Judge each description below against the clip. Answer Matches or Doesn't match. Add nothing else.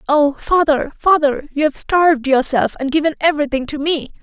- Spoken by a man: Doesn't match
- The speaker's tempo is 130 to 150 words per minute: Doesn't match